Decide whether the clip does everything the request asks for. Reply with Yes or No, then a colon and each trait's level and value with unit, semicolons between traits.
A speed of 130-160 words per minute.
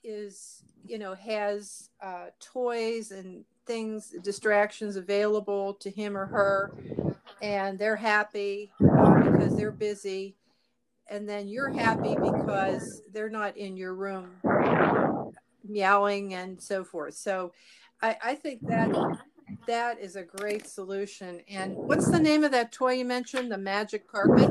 Yes: slow, 135 wpm